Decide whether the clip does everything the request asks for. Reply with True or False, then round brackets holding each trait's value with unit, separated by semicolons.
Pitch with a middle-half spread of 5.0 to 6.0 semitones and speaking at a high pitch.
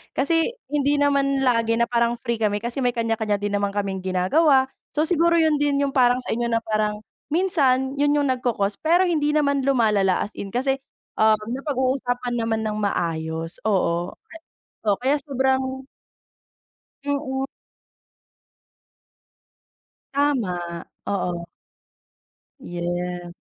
True (5.4 semitones; 245 Hz)